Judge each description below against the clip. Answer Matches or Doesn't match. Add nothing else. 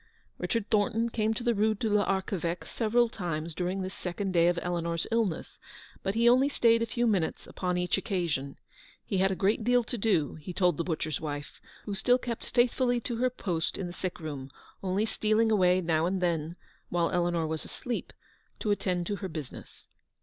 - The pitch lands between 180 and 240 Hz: Matches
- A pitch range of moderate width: Matches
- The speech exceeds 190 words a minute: Matches